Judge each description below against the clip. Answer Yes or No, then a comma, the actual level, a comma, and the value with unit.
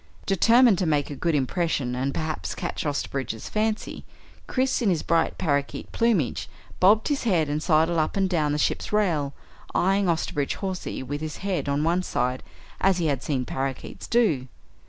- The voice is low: No, medium, 160 Hz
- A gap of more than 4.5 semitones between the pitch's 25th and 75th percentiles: Yes, average, 5.3 semitones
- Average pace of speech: Yes, average, 175 wpm